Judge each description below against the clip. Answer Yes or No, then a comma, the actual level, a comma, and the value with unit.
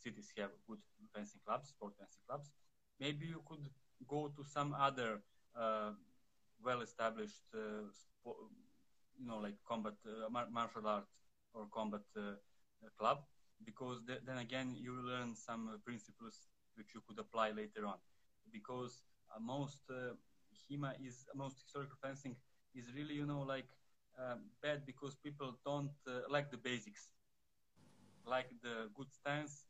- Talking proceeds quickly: No, average, 150 wpm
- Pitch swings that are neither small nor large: Yes, average, 4.1 semitones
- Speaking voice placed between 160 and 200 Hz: No, low, 125 Hz